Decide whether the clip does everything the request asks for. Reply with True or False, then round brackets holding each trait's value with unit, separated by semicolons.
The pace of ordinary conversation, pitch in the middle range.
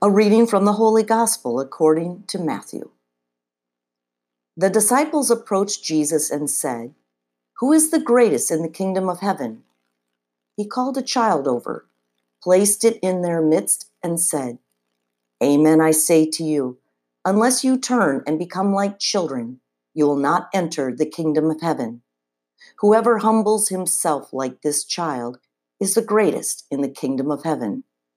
True (150 wpm; 155 Hz)